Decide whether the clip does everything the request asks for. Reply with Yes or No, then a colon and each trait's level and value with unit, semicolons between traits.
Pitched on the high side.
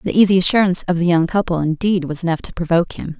No: medium, 175 Hz